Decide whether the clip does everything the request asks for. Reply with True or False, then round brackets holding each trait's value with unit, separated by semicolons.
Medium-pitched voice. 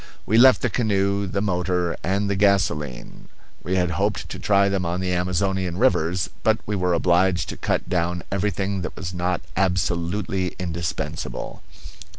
False (95 Hz)